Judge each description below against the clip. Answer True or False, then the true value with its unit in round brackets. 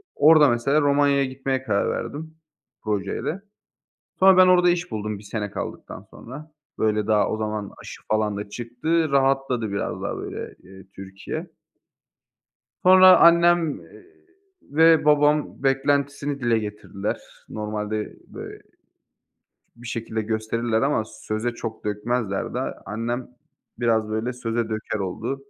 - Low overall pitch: True (120 Hz)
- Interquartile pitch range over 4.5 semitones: True (5.2 semitones)